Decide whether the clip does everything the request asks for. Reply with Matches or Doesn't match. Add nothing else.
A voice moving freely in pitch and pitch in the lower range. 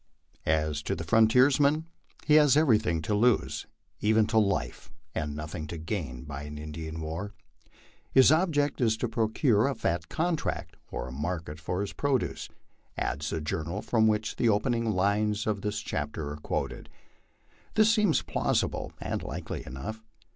Matches